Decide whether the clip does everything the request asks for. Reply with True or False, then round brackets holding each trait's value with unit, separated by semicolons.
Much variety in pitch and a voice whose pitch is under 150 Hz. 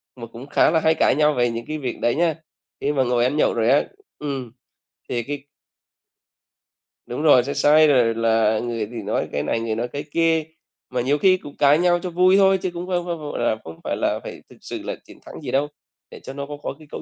False (4.8 semitones; 140 Hz)